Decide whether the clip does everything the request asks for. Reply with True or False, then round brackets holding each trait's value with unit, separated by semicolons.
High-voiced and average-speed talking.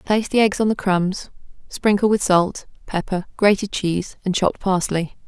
True (195 Hz; 170 wpm)